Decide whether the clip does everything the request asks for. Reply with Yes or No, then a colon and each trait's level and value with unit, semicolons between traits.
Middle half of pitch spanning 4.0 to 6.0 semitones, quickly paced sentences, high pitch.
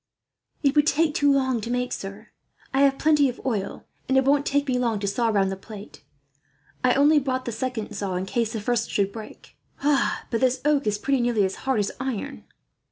Yes: average, 4.5 semitones; fast, 215 wpm; high, 245 Hz